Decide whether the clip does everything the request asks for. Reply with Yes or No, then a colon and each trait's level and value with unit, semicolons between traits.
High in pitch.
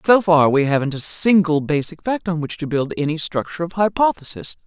No: medium, 165 Hz